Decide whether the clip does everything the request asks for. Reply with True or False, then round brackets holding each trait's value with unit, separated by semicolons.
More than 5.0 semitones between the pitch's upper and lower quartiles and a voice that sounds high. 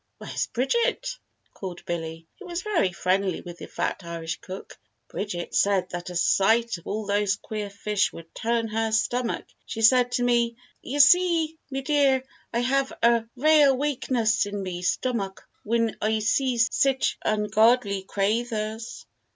False (4.4 semitones; 225 Hz)